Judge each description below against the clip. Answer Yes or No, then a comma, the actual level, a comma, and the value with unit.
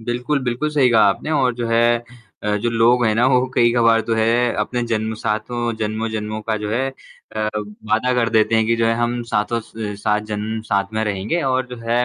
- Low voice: Yes, low, 115 Hz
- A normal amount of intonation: No, narrow, 2.0 semitones